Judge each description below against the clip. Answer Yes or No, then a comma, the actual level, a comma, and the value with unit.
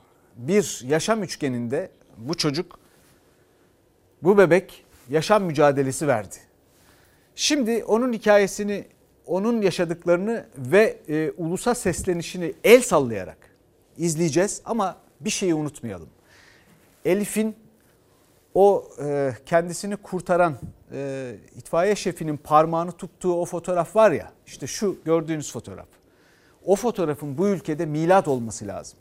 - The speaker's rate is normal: Yes, average, 105 wpm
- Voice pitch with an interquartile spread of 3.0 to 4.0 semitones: No, wide, 5.5 semitones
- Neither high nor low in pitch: Yes, medium, 170 Hz